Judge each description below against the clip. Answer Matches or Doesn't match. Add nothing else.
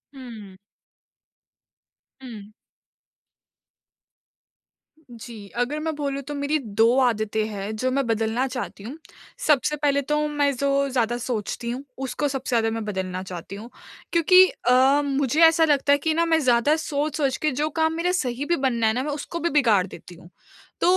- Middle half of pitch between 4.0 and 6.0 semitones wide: Matches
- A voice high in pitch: Matches